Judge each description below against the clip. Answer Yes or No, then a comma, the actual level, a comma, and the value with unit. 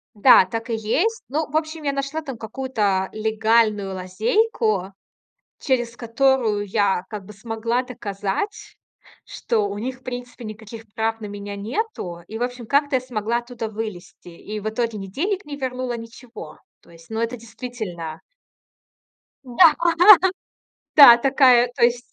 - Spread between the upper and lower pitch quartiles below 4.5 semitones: Yes, average, 3.5 semitones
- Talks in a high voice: Yes, high, 230 Hz